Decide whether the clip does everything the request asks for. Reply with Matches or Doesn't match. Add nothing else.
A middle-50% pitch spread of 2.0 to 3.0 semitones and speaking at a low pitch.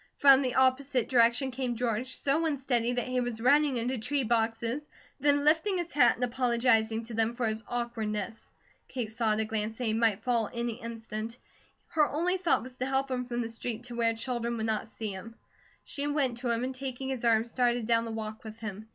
Doesn't match